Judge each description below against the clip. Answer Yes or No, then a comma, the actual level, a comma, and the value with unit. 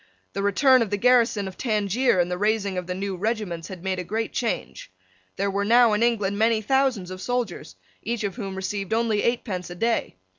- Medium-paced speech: No, fast, 210 wpm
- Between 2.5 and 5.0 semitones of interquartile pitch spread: Yes, average, 3.5 semitones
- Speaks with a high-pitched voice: Yes, high, 205 Hz